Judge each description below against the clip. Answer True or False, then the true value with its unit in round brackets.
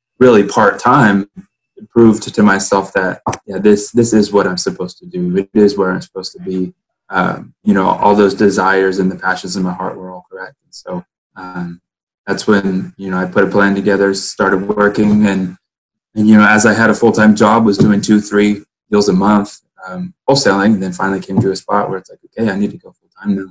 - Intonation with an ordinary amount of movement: False (2.0 semitones)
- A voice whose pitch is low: True (100 Hz)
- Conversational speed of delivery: False (230 wpm)